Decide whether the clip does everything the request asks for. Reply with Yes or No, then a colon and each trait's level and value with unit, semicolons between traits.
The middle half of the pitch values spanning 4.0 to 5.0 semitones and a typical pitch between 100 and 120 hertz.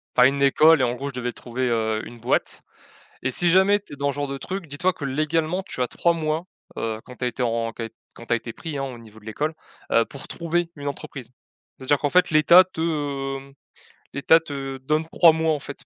No: average, 4.5 semitones; medium, 140 Hz